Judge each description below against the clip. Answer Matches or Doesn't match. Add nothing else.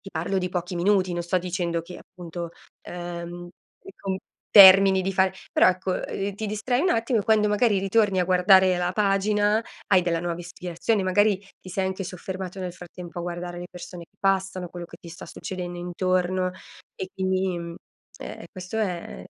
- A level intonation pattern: Matches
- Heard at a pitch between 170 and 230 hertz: Matches